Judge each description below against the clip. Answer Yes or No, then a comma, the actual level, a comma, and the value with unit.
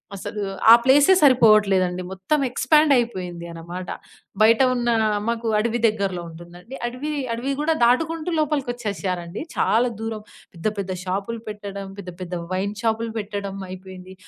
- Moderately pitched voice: No, high, 210 Hz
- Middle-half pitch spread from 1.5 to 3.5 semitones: No, average, 4.5 semitones